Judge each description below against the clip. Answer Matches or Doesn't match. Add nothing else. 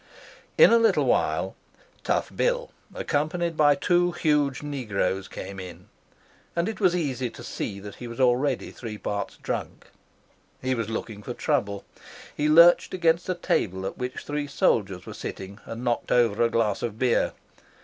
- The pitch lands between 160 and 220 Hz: Doesn't match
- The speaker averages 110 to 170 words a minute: Matches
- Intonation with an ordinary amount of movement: Doesn't match